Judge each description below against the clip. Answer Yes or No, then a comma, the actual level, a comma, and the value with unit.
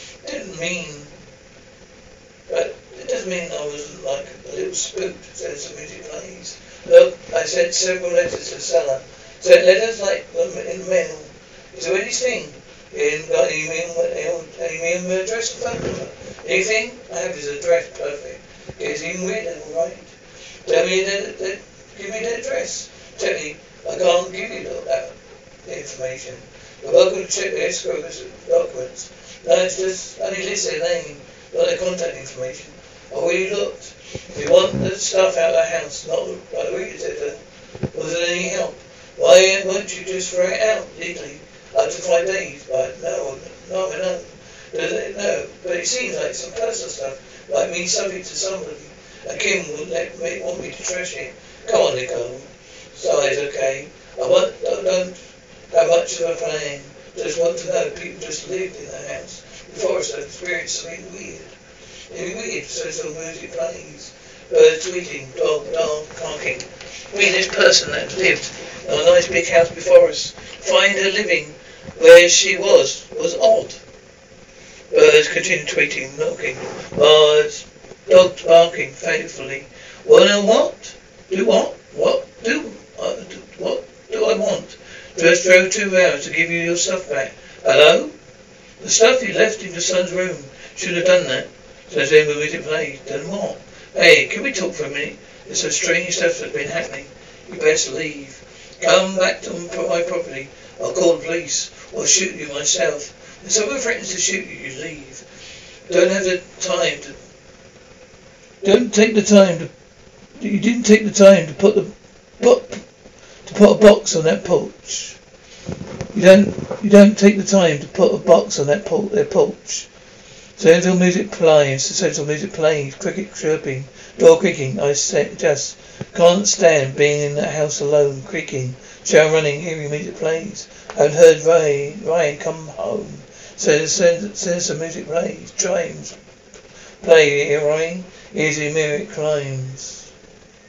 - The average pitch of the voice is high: Yes, high, 195 Hz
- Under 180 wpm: Yes, average, 165 wpm